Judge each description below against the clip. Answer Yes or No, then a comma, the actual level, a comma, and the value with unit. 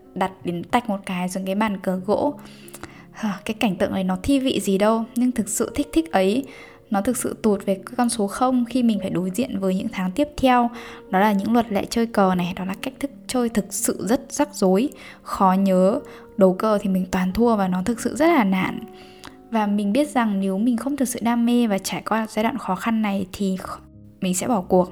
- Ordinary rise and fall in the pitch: Yes, average, 4.0 semitones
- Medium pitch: No, high, 215 Hz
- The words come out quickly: No, average, 240 wpm